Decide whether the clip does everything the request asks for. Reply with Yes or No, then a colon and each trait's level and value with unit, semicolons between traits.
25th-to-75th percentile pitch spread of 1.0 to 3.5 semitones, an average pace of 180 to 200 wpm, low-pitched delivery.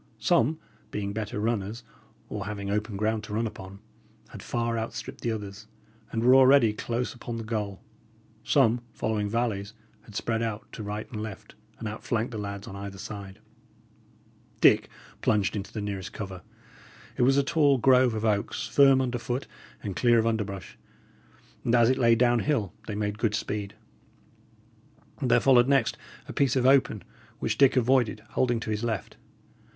No: average, 2.7 semitones; average, 170 wpm; low, 110 Hz